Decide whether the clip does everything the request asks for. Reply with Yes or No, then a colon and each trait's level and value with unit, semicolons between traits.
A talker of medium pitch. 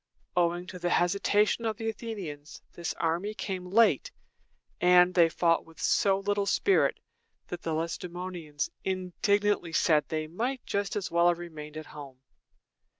Yes: medium, 180 Hz